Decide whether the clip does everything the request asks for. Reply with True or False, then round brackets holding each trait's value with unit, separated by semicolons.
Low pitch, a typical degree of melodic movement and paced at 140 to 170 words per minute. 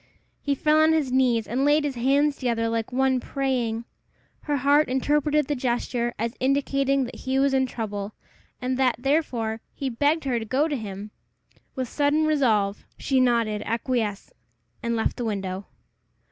False (255 Hz; 3.5 semitones; 165 wpm)